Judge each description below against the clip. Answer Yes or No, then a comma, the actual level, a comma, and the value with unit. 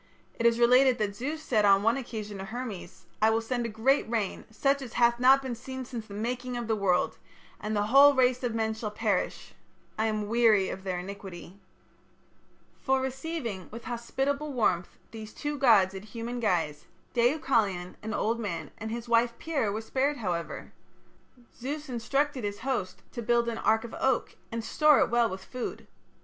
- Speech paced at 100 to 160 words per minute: No, average, 185 wpm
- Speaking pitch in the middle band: No, high, 230 Hz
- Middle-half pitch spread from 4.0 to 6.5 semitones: No, average, 3.5 semitones